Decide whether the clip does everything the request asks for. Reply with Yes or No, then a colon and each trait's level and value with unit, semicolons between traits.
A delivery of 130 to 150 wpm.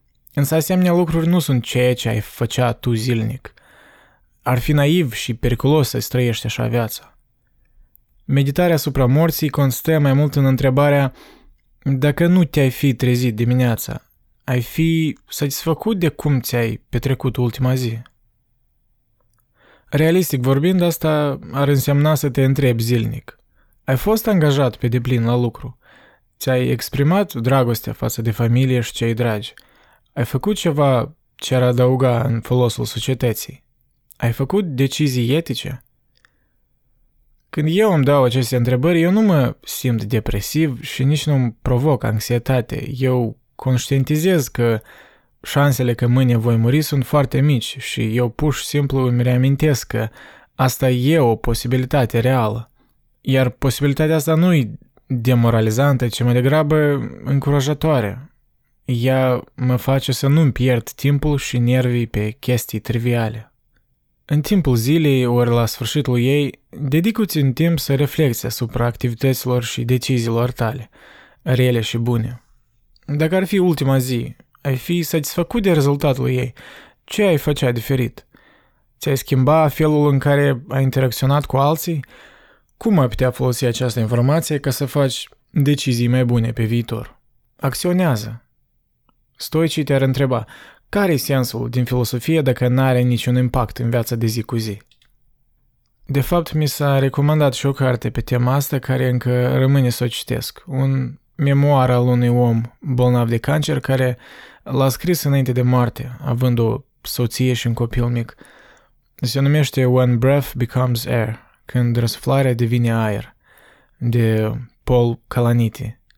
Yes: average, 140 wpm